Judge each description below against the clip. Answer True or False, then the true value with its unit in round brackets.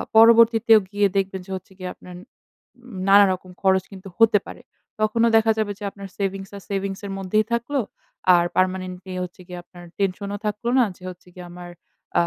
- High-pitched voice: True (195 Hz)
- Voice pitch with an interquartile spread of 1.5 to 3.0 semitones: True (2.7 semitones)